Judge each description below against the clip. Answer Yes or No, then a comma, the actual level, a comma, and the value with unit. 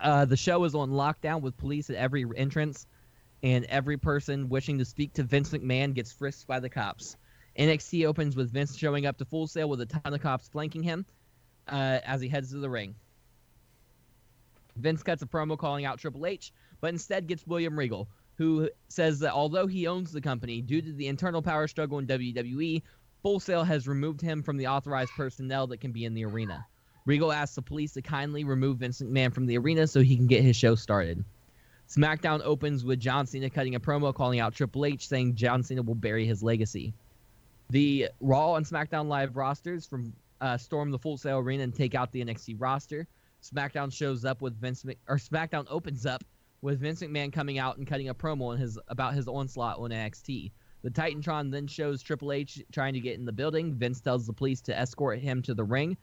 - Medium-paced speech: No, fast, 210 wpm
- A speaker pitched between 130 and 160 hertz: Yes, low, 135 Hz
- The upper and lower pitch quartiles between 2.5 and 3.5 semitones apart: Yes, average, 3.1 semitones